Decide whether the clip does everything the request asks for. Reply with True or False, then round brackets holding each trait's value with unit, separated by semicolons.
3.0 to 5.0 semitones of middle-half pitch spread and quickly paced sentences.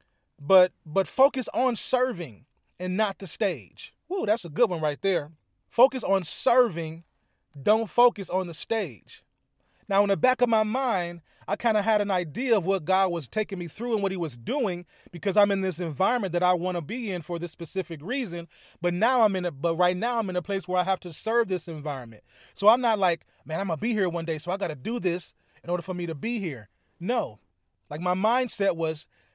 True (4.4 semitones; 225 wpm)